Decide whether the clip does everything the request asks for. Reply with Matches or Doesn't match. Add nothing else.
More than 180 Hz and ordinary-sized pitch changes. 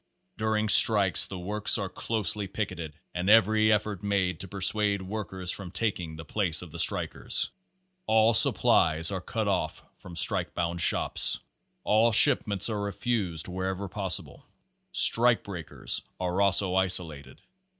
Doesn't match